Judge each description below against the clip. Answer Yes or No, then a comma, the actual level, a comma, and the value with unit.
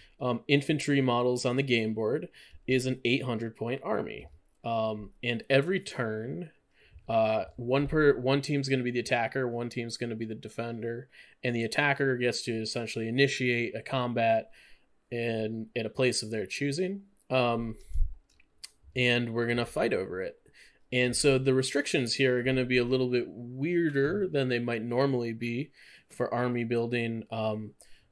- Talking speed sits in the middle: Yes, average, 165 wpm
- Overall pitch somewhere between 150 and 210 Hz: No, low, 120 Hz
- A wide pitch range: No, average, 2.7 semitones